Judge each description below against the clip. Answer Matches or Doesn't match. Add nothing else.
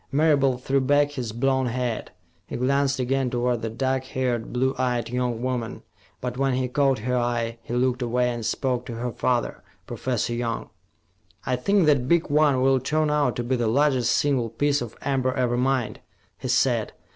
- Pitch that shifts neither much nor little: Doesn't match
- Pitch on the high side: Doesn't match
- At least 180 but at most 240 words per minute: Matches